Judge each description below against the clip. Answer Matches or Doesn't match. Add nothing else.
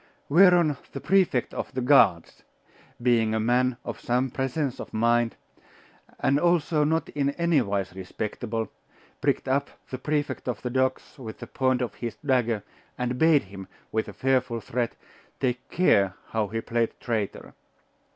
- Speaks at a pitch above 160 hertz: Doesn't match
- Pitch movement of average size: Matches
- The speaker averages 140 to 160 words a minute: Matches